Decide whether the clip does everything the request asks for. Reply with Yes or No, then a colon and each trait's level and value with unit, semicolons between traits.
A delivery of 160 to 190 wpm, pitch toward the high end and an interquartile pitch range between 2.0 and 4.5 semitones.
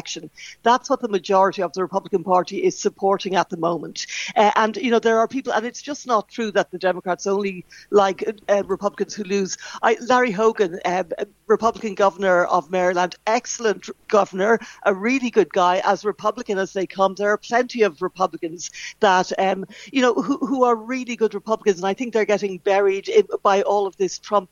No: average, 200 wpm; high, 205 Hz; average, 3.1 semitones